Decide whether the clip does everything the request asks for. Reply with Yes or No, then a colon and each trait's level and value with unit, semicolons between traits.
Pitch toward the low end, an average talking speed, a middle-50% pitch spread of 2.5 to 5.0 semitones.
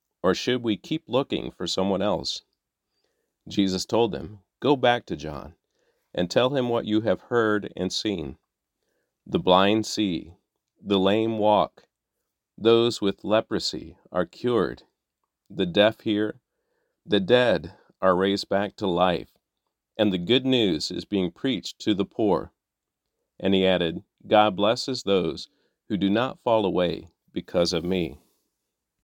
Yes: low, 105 Hz; average, 145 wpm; average, 3.5 semitones